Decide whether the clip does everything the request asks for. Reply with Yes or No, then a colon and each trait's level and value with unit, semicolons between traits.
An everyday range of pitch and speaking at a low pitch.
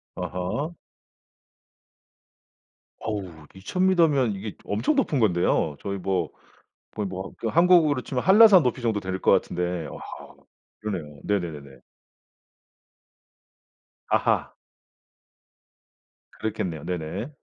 No: wide, 8.1 semitones; low, 100 Hz